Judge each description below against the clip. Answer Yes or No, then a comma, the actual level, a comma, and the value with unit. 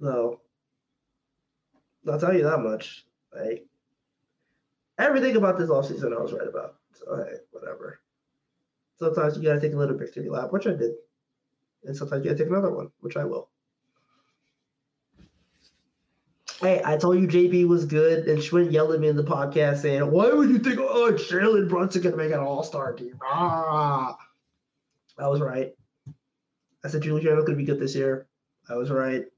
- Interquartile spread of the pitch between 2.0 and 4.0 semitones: No, average, 4.7 semitones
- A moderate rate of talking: Yes, average, 175 wpm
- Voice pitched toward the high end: No, medium, 155 Hz